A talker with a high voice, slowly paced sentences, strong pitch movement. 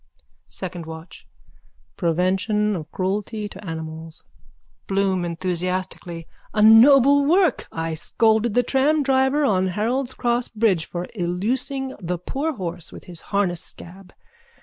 Yes: high, 195 Hz; slow, 125 wpm; wide, 5.8 semitones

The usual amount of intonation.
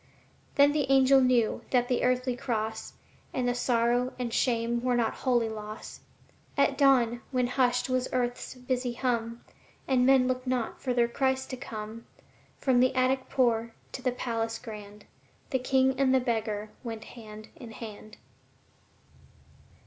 No: narrow, 2.0 semitones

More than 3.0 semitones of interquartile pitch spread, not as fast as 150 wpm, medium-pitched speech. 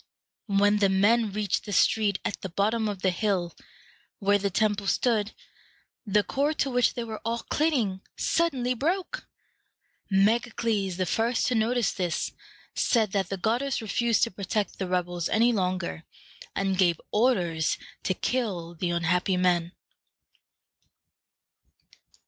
No: average, 3.9 semitones; slow, 135 wpm; high, 205 Hz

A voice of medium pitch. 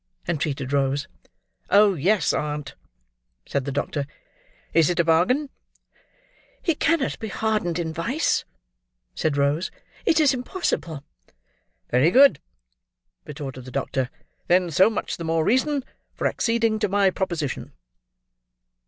Yes: medium, 170 Hz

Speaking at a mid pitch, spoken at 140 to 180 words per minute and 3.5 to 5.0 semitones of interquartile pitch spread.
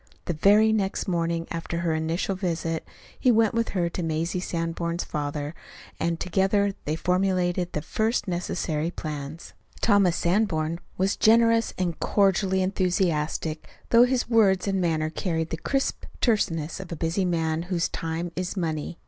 No: medium, 175 Hz; average, 150 wpm; average, 3.1 semitones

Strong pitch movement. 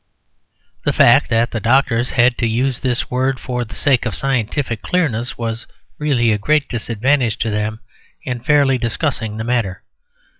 No: average, 2.9 semitones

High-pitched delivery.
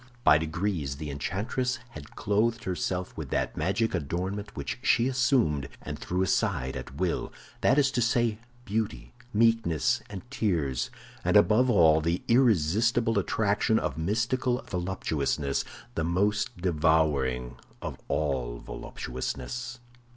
No: very low, 95 Hz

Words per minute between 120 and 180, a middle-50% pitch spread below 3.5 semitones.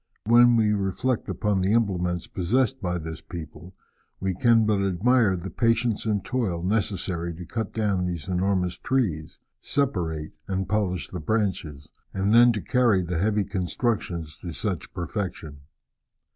No: average, 145 wpm; average, 4.1 semitones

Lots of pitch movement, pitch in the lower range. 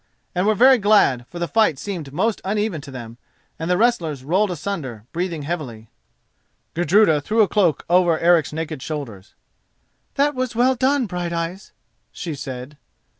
No: wide, 6.2 semitones; medium, 175 Hz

